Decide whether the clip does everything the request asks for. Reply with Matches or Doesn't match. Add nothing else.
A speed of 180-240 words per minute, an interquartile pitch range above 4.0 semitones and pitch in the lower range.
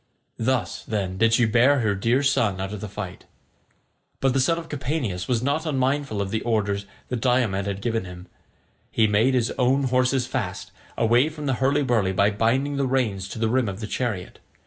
Matches